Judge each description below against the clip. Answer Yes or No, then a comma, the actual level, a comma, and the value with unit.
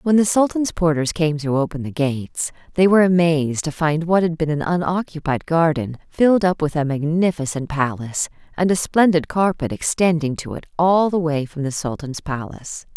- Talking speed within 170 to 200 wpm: Yes, average, 185 wpm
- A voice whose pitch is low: No, medium, 160 Hz